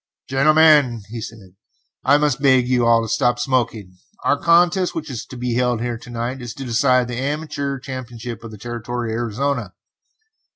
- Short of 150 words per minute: No, average, 180 wpm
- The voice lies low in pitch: Yes, low, 125 Hz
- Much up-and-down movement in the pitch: No, average, 2.9 semitones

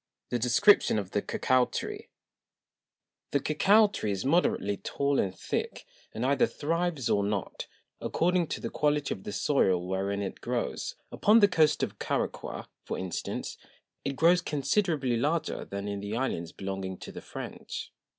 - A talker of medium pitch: No, low, 130 Hz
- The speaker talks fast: No, average, 160 wpm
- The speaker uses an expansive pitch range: Yes, wide, 8.2 semitones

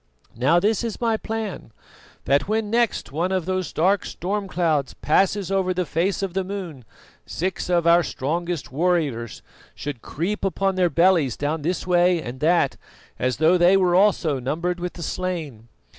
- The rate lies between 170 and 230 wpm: Yes, average, 175 wpm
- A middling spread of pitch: Yes, average, 3.6 semitones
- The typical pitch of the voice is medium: Yes, medium, 175 Hz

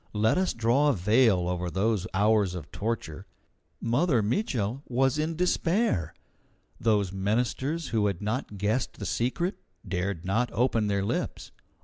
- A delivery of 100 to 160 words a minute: Yes, average, 140 wpm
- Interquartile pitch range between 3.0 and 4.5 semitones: No, average, 4.9 semitones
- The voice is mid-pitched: No, low, 110 Hz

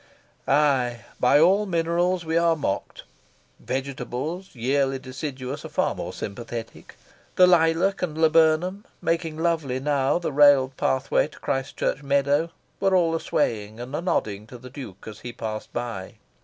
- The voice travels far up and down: No, average, 4.7 semitones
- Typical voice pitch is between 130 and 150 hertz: Yes, medium, 140 Hz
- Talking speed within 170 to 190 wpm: No, average, 155 wpm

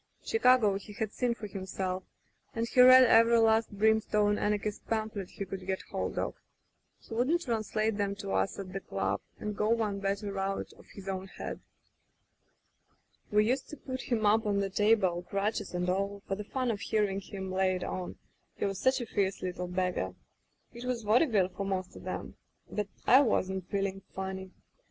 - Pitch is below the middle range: No, high, 205 Hz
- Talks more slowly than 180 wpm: No, average, 190 wpm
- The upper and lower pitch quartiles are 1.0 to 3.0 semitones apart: Yes, average, 2.7 semitones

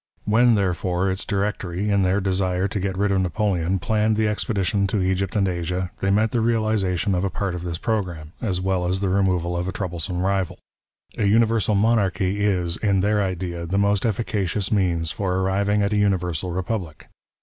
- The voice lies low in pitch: Yes, very low, 95 Hz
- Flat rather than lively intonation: Yes, narrow, 2.3 semitones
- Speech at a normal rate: Yes, average, 190 wpm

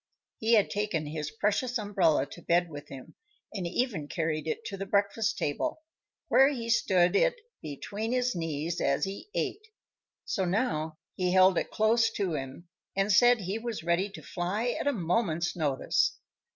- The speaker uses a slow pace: No, average, 170 wpm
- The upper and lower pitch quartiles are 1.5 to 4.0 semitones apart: No, wide, 5.5 semitones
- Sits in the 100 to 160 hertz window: No, high, 195 Hz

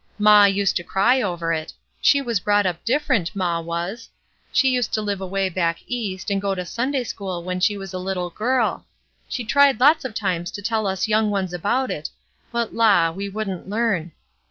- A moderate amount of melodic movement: Yes, average, 4.0 semitones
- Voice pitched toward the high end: Yes, high, 200 Hz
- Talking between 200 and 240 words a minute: Yes, fast, 205 wpm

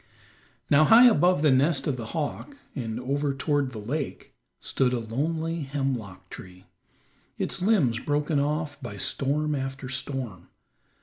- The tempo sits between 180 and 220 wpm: No, average, 140 wpm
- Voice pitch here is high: No, medium, 140 Hz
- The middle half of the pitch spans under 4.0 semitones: Yes, average, 3.4 semitones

